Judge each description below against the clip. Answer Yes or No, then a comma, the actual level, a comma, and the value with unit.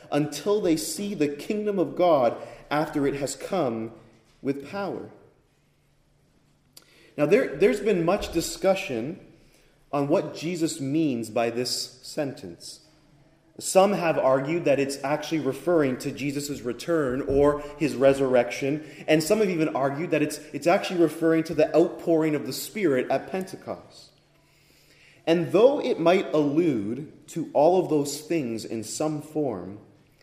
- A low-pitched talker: No, medium, 150 Hz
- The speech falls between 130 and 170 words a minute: Yes, average, 140 wpm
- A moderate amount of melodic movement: Yes, average, 3.1 semitones